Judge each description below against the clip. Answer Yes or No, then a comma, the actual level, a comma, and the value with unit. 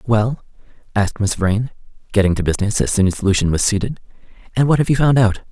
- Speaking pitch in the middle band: No, low, 110 Hz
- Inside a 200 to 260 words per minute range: Yes, fast, 205 wpm